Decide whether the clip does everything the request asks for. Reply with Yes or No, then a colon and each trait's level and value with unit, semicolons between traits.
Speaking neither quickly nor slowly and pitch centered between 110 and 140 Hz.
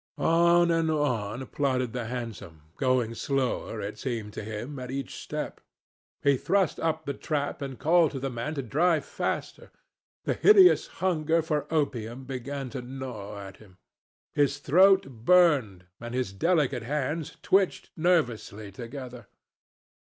Yes: average, 145 wpm; low, 135 Hz